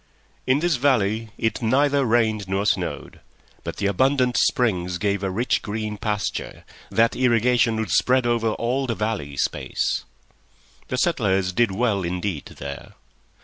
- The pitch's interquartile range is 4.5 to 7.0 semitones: No, average, 3.9 semitones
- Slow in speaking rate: No, average, 145 wpm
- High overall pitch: No, low, 110 Hz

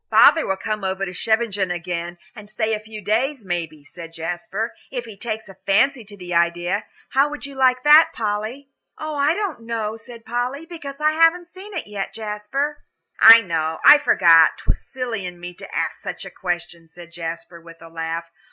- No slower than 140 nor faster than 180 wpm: No, average, 190 wpm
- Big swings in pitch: Yes, wide, 7.1 semitones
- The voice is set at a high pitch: Yes, high, 215 Hz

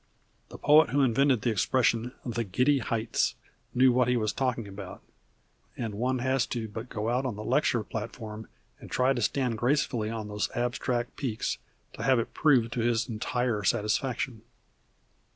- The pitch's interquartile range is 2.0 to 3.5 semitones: Yes, narrow, 2.6 semitones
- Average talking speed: Yes, average, 170 wpm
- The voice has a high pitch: No, low, 120 Hz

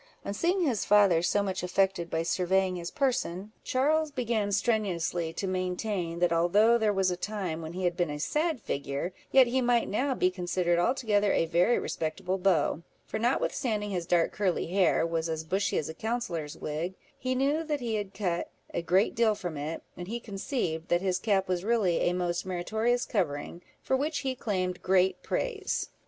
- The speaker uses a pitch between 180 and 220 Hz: Yes, high, 190 Hz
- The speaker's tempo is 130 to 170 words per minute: No, average, 190 wpm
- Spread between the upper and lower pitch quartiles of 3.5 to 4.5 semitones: No, average, 4.9 semitones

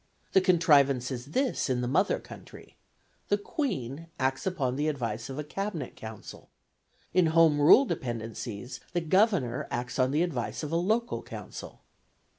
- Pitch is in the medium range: Yes, medium, 145 Hz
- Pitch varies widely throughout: Yes, wide, 6.2 semitones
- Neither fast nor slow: Yes, average, 155 wpm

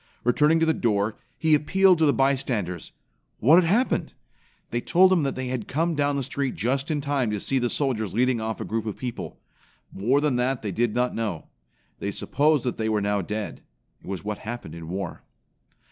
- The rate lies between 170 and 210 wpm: Yes, fast, 205 wpm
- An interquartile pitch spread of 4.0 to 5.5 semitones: Yes, average, 5.2 semitones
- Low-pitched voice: Yes, low, 125 Hz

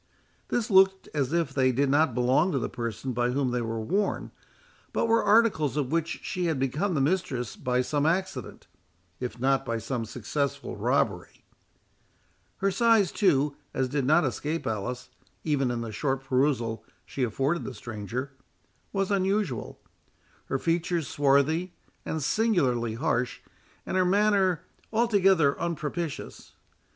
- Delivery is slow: No, average, 145 wpm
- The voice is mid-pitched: Yes, medium, 145 Hz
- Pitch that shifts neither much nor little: No, wide, 6.2 semitones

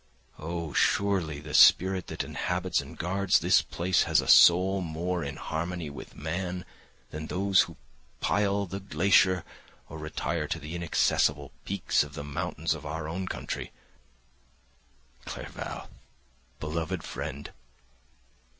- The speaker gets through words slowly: Yes, slow, 130 wpm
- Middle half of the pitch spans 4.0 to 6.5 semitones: No, average, 3.3 semitones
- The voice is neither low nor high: No, very low, 85 Hz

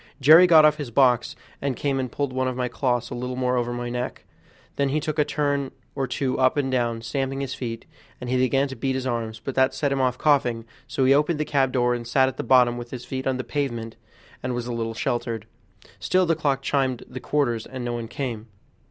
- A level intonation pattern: Yes, narrow, 2.3 semitones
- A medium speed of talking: No, fast, 245 wpm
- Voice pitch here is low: Yes, low, 130 Hz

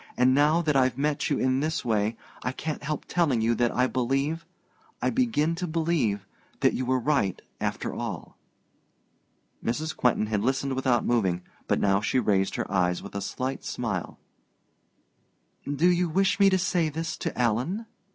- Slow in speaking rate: No, average, 170 wpm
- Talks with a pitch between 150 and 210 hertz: No, low, 130 Hz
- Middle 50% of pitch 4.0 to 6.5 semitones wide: Yes, wide, 5.6 semitones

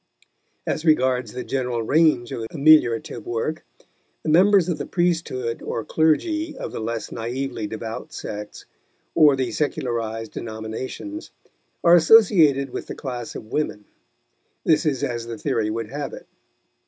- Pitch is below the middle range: Yes, low, 130 Hz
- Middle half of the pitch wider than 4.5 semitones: Yes, wide, 5.4 semitones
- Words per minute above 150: No, average, 140 wpm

